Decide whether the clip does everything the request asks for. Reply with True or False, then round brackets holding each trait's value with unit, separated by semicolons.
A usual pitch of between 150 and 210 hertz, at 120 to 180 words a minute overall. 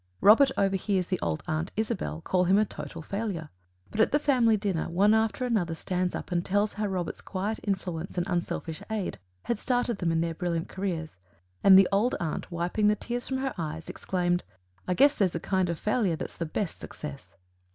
False (190 Hz; 200 wpm)